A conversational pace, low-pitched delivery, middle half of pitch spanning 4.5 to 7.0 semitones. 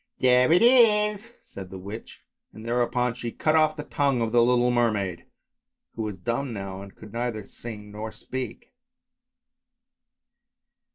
Yes: average, 155 wpm; low, 120 Hz; average, 4.8 semitones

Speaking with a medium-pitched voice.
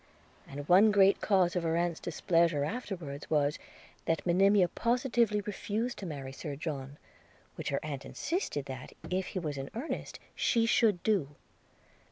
Yes: medium, 175 Hz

